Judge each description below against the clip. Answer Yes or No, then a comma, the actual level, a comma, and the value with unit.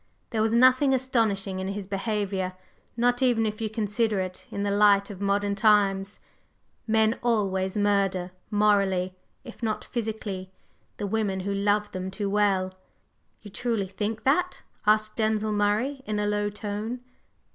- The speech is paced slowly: No, average, 150 wpm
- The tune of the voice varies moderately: No, narrow, 2.0 semitones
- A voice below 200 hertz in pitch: No, high, 210 Hz